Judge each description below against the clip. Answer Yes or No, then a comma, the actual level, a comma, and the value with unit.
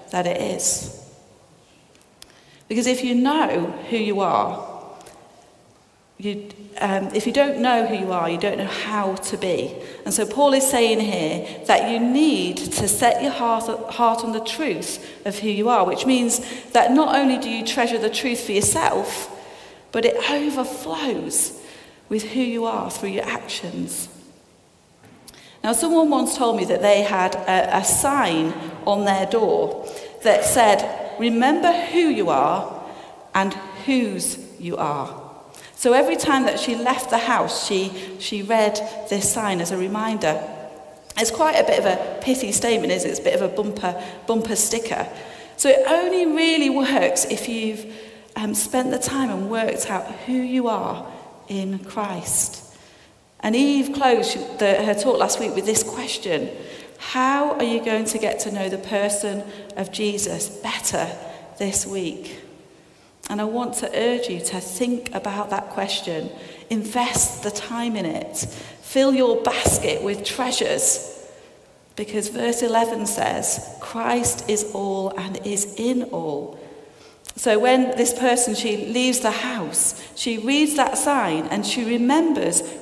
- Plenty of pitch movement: No, average, 4.1 semitones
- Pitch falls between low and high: No, high, 230 Hz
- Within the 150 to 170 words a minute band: Yes, average, 160 wpm